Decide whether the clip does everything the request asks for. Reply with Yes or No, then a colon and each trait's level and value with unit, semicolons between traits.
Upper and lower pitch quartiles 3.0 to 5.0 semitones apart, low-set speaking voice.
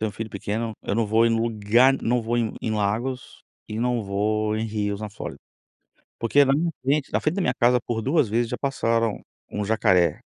No: narrow, 2.5 semitones; low, 115 Hz